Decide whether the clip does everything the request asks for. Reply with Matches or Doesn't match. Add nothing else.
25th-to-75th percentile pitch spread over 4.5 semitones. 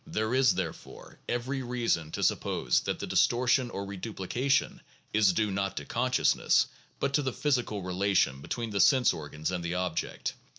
Matches